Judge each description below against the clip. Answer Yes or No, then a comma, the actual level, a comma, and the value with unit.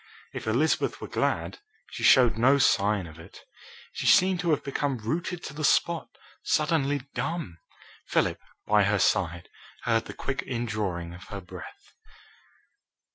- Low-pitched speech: Yes, low, 120 Hz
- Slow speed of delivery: No, average, 145 wpm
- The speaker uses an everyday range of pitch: No, wide, 6.9 semitones